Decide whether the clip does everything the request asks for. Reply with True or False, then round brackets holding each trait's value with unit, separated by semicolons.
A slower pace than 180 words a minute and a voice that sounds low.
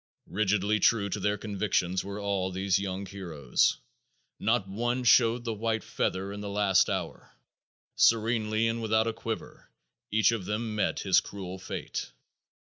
True (150 wpm; 105 Hz)